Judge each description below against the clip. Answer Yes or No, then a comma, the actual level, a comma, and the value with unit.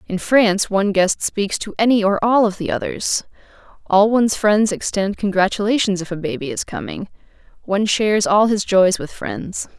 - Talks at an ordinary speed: Yes, average, 180 wpm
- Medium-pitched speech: No, high, 200 Hz